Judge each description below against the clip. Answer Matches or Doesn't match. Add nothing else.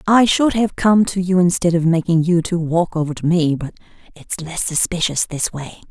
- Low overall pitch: Doesn't match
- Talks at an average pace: Doesn't match